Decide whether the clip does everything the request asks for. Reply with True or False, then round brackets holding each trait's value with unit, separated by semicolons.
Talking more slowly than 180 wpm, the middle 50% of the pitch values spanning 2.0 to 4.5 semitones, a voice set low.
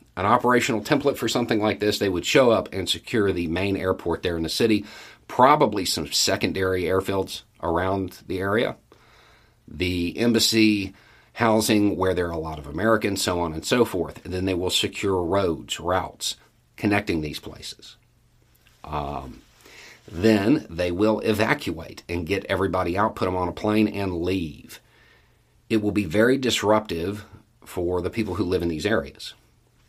True (165 wpm; 3.5 semitones; 100 Hz)